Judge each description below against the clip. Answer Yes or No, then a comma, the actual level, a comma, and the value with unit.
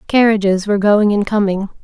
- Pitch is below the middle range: No, high, 205 Hz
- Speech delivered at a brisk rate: No, average, 165 wpm